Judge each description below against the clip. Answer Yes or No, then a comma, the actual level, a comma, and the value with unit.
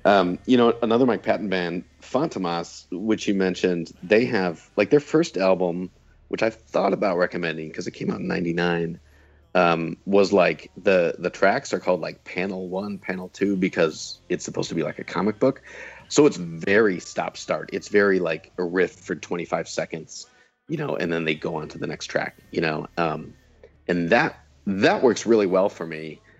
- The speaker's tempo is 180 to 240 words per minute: Yes, average, 195 wpm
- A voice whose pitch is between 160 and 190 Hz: No, very low, 90 Hz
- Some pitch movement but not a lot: Yes, average, 3.0 semitones